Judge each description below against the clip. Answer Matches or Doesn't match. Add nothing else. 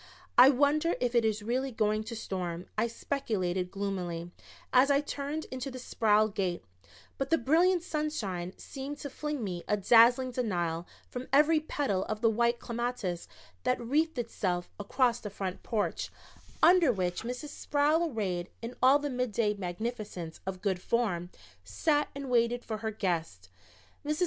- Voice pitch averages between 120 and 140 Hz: Doesn't match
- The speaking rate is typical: Matches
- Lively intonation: Matches